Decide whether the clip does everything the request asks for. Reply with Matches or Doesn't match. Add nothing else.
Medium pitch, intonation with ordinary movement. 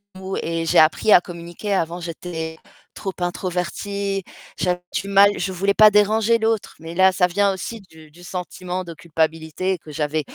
Matches